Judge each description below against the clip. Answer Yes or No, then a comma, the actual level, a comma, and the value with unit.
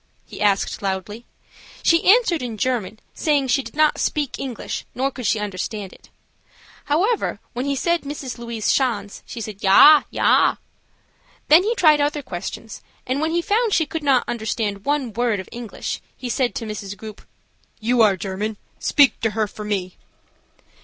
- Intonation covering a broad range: Yes, wide, 5.7 semitones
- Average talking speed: Yes, average, 170 wpm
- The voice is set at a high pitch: Yes, high, 240 Hz